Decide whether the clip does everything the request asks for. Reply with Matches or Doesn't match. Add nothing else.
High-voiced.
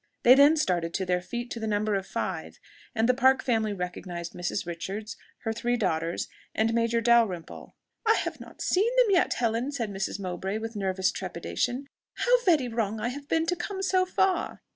Matches